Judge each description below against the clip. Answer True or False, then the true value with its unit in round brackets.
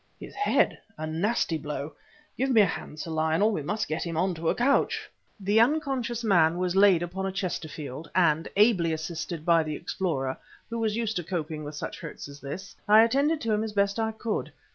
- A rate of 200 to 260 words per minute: True (205 wpm)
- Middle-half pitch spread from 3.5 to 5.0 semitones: False (5.5 semitones)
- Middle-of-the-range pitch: True (180 Hz)